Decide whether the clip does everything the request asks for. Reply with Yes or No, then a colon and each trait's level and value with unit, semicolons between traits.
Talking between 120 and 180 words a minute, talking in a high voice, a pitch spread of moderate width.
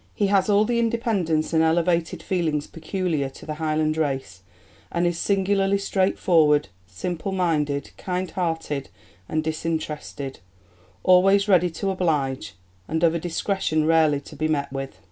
No: average, 145 wpm; medium, 165 Hz; average, 3.6 semitones